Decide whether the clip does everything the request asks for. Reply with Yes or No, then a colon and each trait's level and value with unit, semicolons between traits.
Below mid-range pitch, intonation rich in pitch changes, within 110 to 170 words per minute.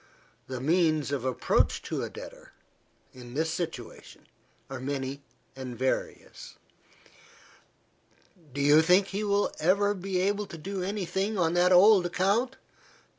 No: medium, 175 Hz; wide, 5.9 semitones; slow, 135 wpm